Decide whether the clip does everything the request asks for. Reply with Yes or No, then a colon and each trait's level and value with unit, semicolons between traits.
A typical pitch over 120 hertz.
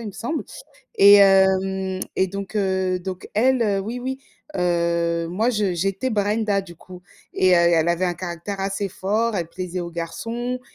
Yes: high, 190 Hz